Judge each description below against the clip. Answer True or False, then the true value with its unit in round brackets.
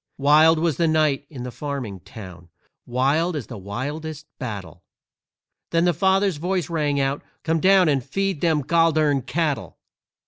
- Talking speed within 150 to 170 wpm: True (160 wpm)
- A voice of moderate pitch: True (150 Hz)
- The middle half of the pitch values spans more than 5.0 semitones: False (4.0 semitones)